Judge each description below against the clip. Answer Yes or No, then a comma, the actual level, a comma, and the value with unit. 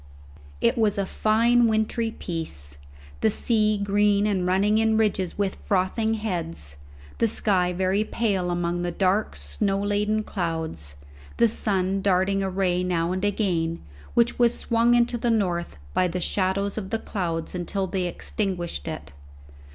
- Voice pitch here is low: No, high, 195 Hz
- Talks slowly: No, average, 150 wpm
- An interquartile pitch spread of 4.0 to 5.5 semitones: No, average, 3.4 semitones